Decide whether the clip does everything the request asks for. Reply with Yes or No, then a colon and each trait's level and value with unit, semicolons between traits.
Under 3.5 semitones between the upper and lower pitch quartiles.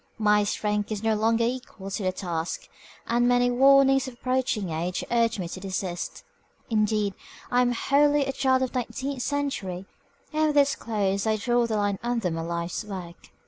No: average, 4.6 semitones